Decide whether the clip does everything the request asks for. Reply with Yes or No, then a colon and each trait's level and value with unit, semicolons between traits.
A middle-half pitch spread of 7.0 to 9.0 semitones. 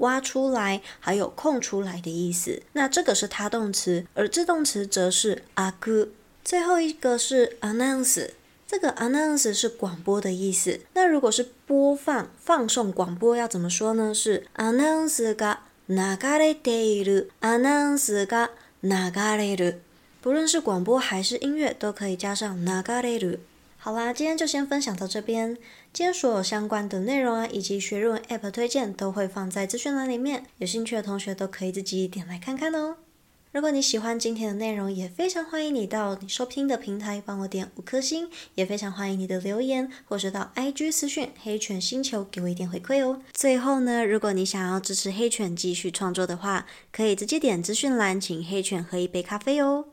No: average, 5.3 semitones